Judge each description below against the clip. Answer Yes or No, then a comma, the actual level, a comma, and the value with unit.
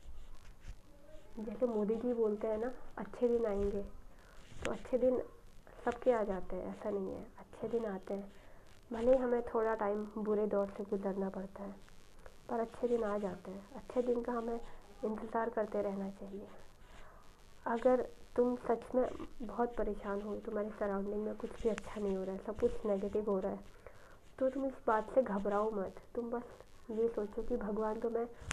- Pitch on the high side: Yes, high, 220 Hz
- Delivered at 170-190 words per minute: Yes, average, 180 wpm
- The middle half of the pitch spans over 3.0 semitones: No, average, 2.7 semitones